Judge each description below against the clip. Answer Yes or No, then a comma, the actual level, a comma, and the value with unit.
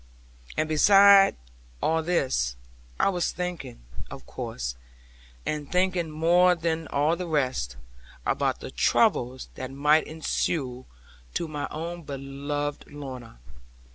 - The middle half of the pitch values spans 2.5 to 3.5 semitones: No, average, 4.0 semitones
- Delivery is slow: Yes, slow, 115 wpm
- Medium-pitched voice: Yes, medium, 155 Hz